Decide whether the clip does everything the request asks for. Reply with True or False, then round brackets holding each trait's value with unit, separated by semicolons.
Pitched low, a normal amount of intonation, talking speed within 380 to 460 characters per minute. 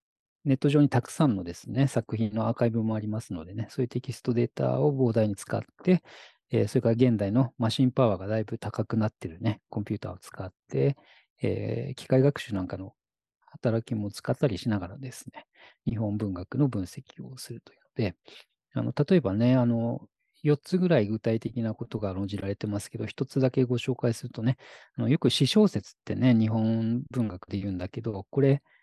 True (115 Hz; 3.4 semitones; 385 characters per minute)